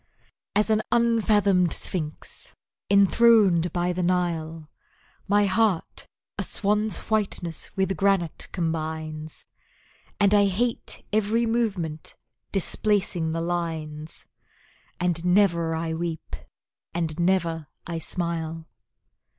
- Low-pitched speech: No, medium, 175 Hz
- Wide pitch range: No, average, 3.8 semitones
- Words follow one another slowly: Yes, slow, 100 wpm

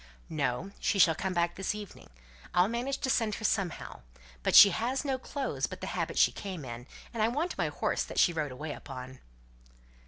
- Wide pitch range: Yes, wide, 7.0 semitones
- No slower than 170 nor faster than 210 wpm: Yes, average, 200 wpm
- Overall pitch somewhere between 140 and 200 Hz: Yes, high, 190 Hz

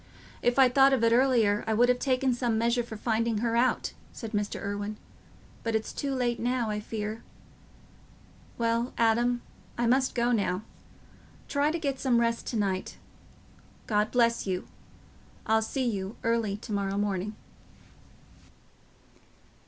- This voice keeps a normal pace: Yes, average, 150 wpm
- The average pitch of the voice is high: Yes, high, 230 Hz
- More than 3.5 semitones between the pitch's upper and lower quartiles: No, narrow, 2.6 semitones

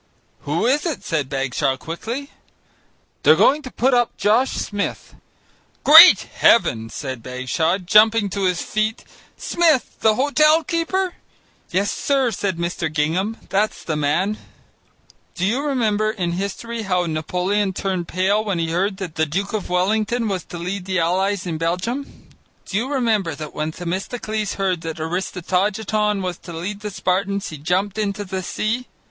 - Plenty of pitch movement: No, average, 4.2 semitones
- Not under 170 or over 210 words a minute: No, average, 155 wpm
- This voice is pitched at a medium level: No, high, 195 Hz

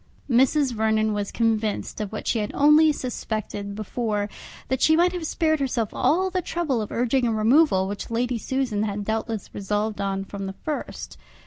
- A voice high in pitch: Yes, high, 225 Hz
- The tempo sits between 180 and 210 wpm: Yes, average, 185 wpm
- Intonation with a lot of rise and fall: No, average, 4.6 semitones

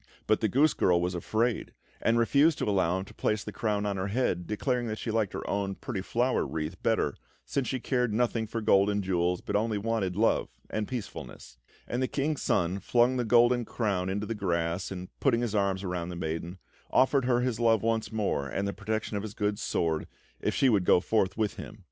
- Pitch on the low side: Yes, low, 105 Hz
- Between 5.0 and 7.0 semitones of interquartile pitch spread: No, average, 3.8 semitones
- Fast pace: Yes, fast, 220 wpm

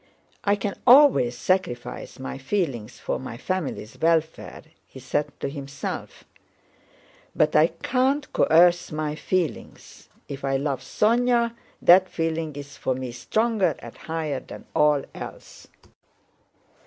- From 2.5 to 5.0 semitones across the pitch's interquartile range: No, wide, 5.6 semitones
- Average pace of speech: No, slow, 125 wpm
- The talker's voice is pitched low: No, medium, 160 Hz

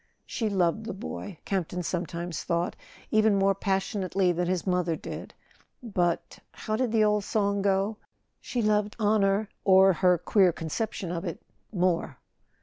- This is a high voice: Yes, high, 195 Hz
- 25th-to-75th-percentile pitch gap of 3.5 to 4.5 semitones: No, average, 2.8 semitones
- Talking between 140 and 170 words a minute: Yes, average, 145 wpm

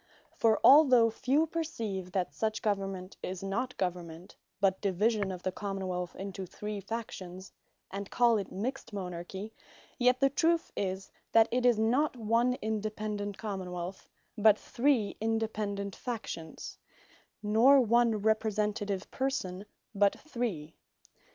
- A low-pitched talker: No, high, 210 Hz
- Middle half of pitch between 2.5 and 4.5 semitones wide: Yes, average, 3.5 semitones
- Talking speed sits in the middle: No, slow, 130 wpm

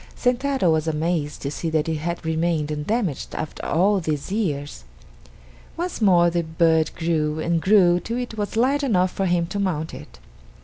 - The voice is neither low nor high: Yes, medium, 170 Hz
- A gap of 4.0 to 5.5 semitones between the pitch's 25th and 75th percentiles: Yes, average, 4.3 semitones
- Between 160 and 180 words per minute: Yes, average, 175 wpm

